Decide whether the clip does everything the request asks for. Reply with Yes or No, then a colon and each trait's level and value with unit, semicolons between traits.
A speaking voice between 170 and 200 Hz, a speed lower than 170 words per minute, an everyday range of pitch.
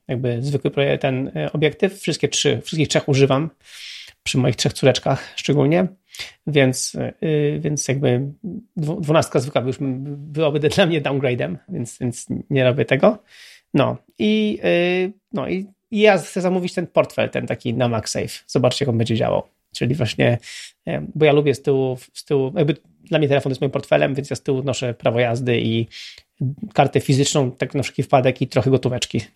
No: medium, 140 Hz; fast, 160 wpm; average, 3.9 semitones